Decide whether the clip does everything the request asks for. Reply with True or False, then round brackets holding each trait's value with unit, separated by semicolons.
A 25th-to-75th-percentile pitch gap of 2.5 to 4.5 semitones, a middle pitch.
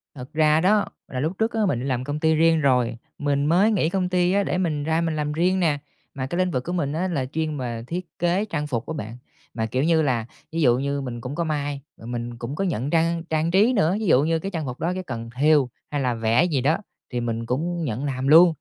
False (5.0 semitones; 150 Hz)